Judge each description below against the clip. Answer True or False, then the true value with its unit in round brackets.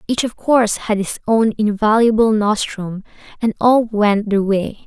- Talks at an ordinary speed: True (160 wpm)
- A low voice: False (215 Hz)